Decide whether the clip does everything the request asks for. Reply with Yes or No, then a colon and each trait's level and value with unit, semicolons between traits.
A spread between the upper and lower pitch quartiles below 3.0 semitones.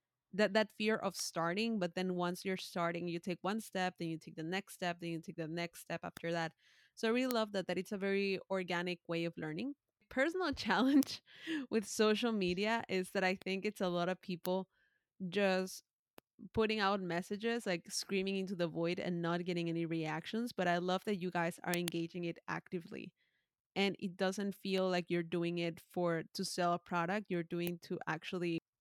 Yes: narrow, 2.5 semitones